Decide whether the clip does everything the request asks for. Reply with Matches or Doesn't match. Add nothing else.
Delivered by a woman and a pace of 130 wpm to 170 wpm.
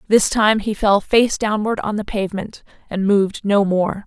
Doesn't match